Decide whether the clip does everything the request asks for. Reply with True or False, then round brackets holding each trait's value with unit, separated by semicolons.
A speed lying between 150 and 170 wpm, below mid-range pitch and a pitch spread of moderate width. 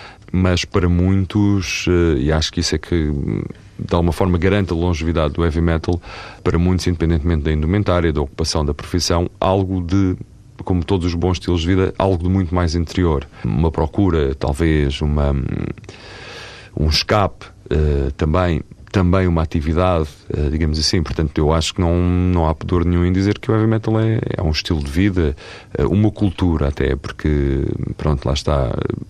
True (165 wpm; 85 Hz; 3.2 semitones)